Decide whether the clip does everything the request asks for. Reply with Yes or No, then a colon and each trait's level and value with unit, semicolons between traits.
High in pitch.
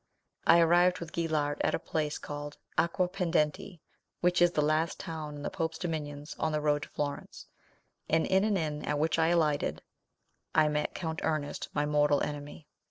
No: medium, 155 Hz